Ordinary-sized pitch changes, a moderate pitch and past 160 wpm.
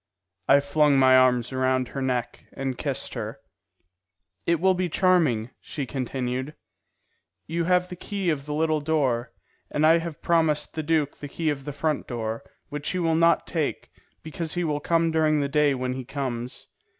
Yes: average, 3.8 semitones; medium, 150 Hz; average, 180 wpm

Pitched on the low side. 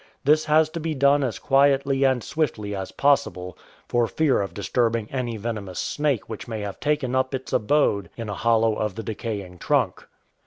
Yes: low, 120 Hz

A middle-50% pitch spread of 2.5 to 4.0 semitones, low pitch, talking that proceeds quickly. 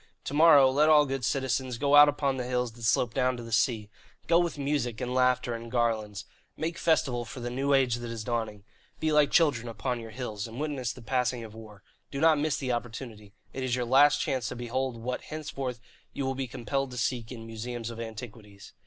Yes: average, 3.0 semitones; low, 125 Hz; fast, 220 wpm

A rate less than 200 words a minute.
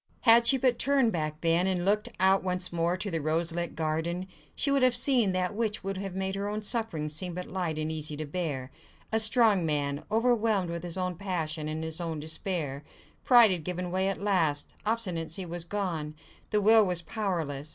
No: fast, 205 wpm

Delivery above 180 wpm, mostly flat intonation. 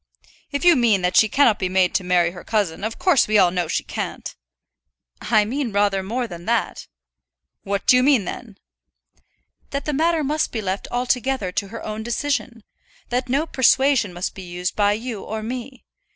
No: average, 190 wpm; average, 5.1 semitones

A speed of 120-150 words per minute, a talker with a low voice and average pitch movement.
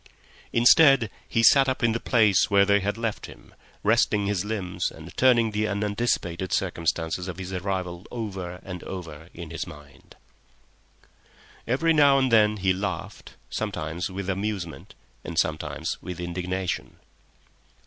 Yes: average, 140 wpm; low, 100 Hz; average, 3.9 semitones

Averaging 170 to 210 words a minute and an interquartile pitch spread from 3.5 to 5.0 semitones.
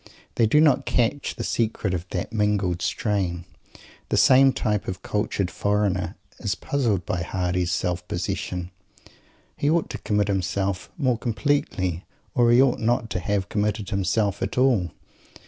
No: average, 155 wpm; average, 4.2 semitones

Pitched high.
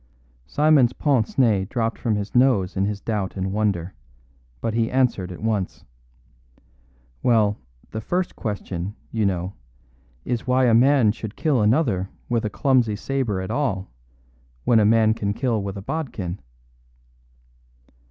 No: low, 110 Hz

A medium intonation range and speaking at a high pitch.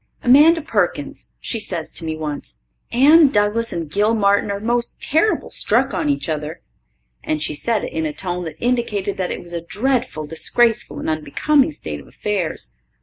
No: wide, 7.1 semitones; high, 200 Hz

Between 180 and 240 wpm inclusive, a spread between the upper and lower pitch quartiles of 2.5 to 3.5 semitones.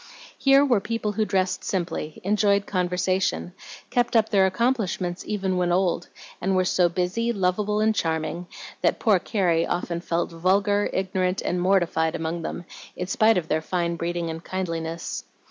No: average, 160 wpm; average, 2.9 semitones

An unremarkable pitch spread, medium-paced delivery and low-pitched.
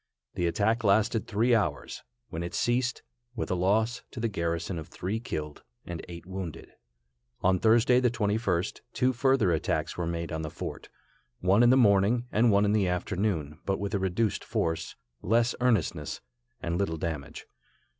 Yes: average, 5.0 semitones; average, 170 wpm; low, 100 Hz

